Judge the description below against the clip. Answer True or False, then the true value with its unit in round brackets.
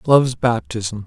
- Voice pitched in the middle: False (115 Hz)